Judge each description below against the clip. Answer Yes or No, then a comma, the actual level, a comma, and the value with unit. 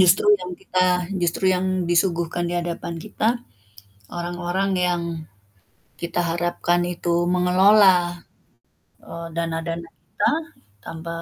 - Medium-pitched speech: Yes, medium, 175 Hz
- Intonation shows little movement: Yes, narrow, 1.2 semitones